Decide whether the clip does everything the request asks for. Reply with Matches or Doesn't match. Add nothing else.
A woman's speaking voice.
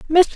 Matches